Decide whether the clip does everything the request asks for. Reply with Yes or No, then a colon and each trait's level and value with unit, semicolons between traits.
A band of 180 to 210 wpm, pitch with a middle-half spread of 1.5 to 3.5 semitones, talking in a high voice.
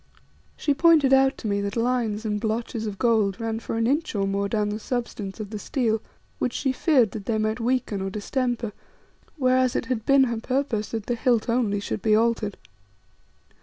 Yes: average, 200 wpm; average, 3.2 semitones; high, 225 Hz